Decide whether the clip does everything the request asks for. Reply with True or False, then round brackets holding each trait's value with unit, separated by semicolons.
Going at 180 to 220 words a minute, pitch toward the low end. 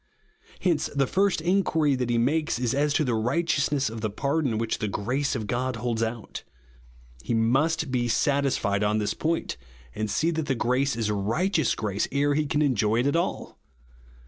True (185 wpm; 130 Hz)